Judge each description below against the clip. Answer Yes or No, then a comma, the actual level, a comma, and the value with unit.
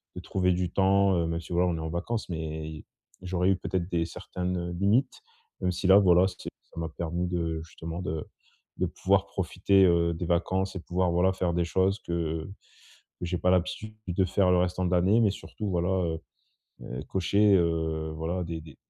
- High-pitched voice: No, very low, 90 Hz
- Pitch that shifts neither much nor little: No, narrow, 2.2 semitones